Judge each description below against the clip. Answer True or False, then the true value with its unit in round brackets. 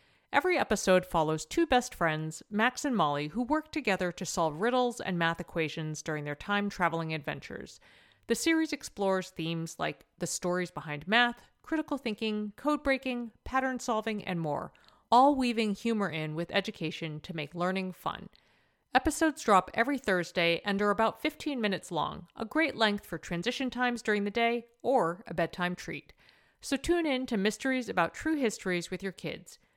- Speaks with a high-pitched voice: True (205 Hz)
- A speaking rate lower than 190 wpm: True (170 wpm)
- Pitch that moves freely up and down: True (6.5 semitones)